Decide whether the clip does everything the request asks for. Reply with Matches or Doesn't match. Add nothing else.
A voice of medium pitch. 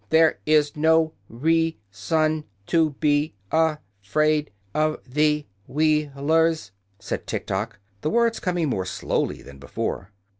Matches